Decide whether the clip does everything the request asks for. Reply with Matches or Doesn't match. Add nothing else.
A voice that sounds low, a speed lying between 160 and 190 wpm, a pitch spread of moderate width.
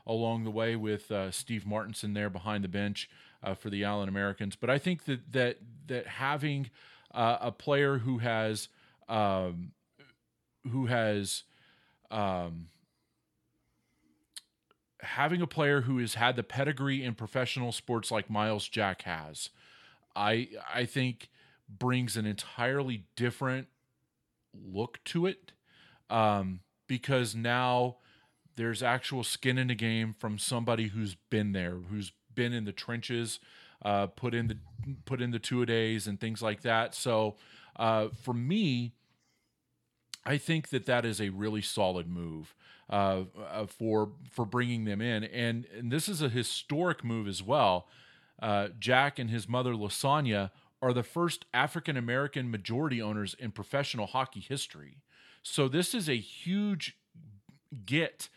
Doesn't match